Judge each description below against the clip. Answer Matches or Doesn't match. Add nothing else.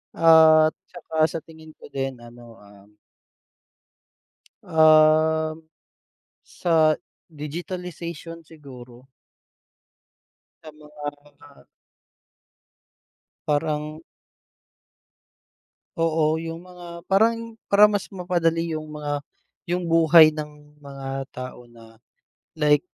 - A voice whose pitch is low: Doesn't match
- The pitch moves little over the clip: Matches